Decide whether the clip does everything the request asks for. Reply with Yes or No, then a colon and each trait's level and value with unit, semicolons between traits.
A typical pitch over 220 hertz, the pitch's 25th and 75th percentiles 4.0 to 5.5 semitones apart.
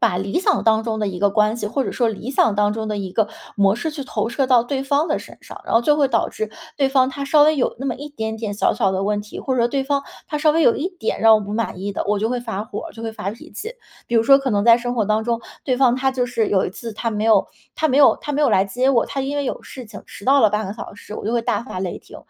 Yes: high, 230 Hz; average, 4.3 semitones